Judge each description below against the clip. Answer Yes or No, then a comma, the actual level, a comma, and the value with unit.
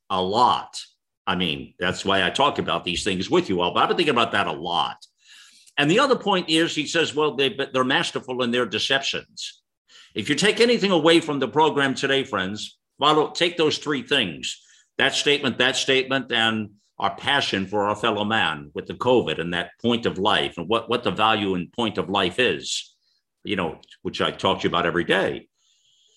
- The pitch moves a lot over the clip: Yes, wide, 5.9 semitones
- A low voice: Yes, low, 130 Hz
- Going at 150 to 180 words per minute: No, fast, 205 wpm